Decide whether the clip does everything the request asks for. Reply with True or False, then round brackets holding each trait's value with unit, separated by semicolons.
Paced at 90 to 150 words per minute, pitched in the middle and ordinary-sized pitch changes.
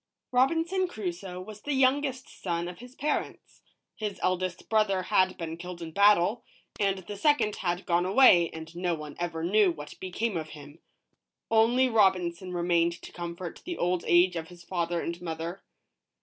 False (165 wpm; 180 Hz; 4.0 semitones)